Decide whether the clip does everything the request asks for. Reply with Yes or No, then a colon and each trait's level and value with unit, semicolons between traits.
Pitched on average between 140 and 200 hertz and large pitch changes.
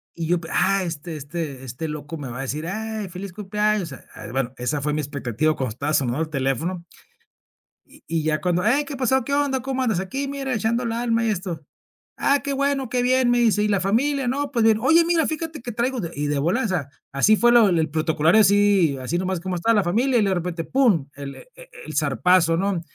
Yes: high, 190 Hz; wide, 7.4 semitones